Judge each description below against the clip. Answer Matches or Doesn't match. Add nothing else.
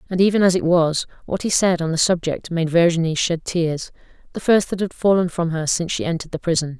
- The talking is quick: Matches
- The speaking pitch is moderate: Matches